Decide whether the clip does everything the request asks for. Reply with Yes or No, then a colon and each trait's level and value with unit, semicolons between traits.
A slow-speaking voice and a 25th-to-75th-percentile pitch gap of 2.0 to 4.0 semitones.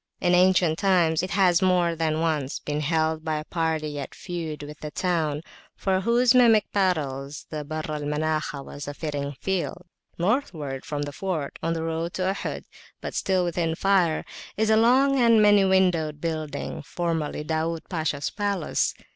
No: average, 165 wpm; average, 3.6 semitones